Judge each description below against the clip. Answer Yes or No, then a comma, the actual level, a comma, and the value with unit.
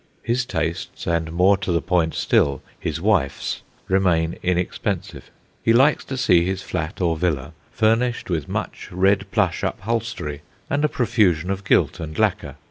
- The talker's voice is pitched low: Yes, very low, 90 Hz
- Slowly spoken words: No, average, 155 wpm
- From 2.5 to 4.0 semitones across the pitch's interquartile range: No, average, 4.7 semitones